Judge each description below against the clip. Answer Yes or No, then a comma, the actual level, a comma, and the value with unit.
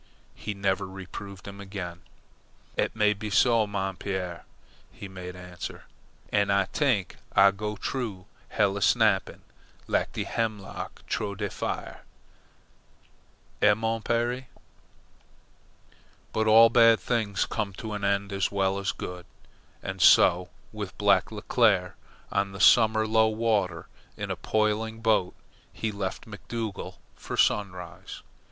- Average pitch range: No, narrow, 2.3 semitones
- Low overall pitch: Yes, low, 100 Hz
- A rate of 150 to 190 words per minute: No, slow, 135 wpm